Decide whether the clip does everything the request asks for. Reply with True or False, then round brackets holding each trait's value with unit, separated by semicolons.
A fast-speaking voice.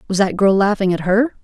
True (250 wpm)